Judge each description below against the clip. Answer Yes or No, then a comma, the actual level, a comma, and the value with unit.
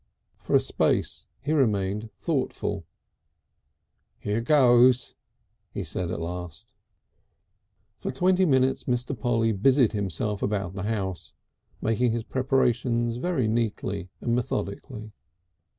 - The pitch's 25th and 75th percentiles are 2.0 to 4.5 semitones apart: Yes, average, 4.2 semitones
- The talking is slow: Yes, slow, 115 wpm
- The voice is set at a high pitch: No, low, 115 Hz